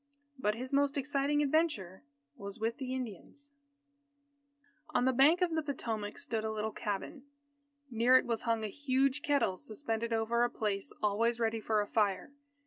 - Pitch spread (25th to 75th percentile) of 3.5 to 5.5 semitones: Yes, average, 4.3 semitones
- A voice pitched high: Yes, high, 235 Hz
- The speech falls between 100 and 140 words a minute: No, average, 160 wpm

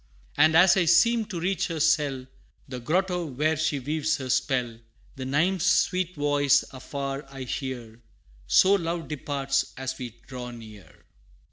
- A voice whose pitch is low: No, medium, 145 Hz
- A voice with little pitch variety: No, average, 4.3 semitones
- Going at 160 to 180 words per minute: No, average, 150 wpm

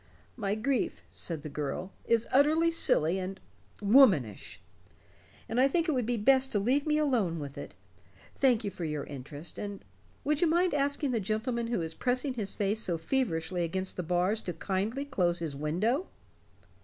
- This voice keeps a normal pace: Yes, average, 175 wpm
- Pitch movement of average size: No, wide, 7.5 semitones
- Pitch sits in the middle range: No, high, 215 Hz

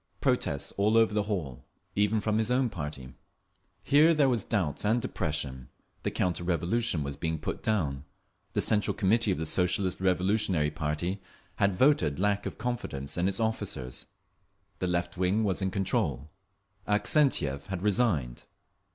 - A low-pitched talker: Yes, very low, 95 Hz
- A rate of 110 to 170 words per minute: Yes, average, 150 wpm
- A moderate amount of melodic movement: No, wide, 5.7 semitones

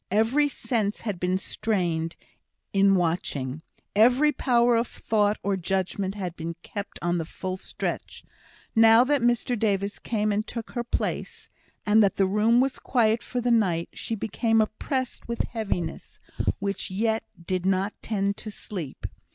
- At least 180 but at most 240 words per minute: No, average, 155 wpm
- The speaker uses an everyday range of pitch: Yes, average, 3.5 semitones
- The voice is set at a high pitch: Yes, high, 210 Hz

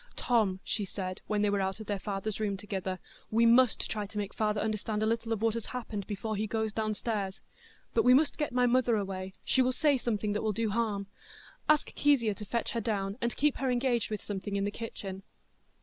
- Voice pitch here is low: No, high, 215 Hz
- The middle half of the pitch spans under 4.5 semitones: Yes, average, 2.7 semitones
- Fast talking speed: Yes, fast, 225 wpm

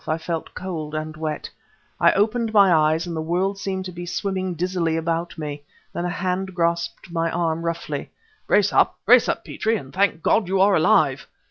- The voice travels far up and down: No, average, 2.9 semitones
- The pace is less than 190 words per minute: No, average, 195 wpm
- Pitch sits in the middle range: Yes, medium, 175 Hz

